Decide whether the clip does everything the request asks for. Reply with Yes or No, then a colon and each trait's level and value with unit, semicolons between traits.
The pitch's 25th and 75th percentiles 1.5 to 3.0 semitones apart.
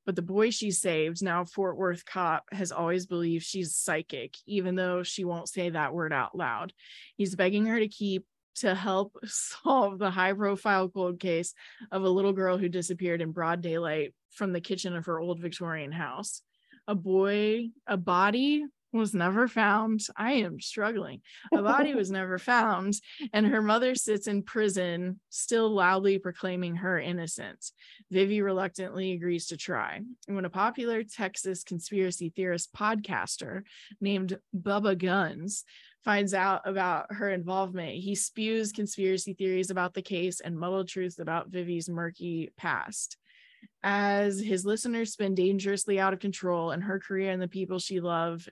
Yes: narrow, 2.4 semitones